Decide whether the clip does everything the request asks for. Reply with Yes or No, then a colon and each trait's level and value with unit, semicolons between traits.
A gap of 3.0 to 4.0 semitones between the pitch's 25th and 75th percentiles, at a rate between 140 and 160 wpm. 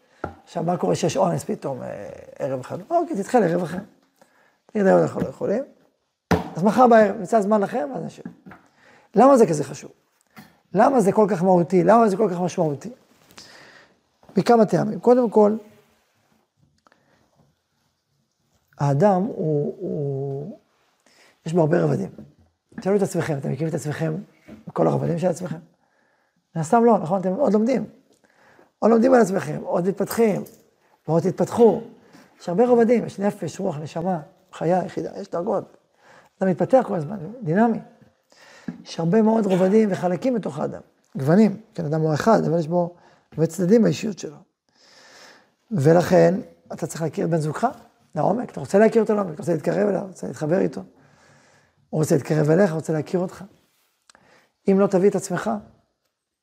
No: average, 4.6 semitones; fast, 150 wpm